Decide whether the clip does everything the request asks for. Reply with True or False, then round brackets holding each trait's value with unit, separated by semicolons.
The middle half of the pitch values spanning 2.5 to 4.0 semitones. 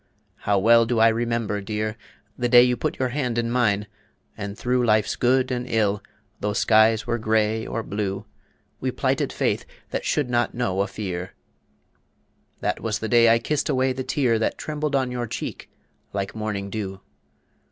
True (2.8 semitones)